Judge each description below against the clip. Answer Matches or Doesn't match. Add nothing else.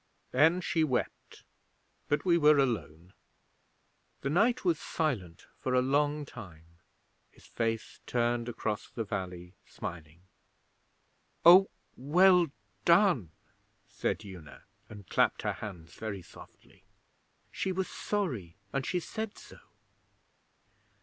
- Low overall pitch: Matches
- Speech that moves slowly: Matches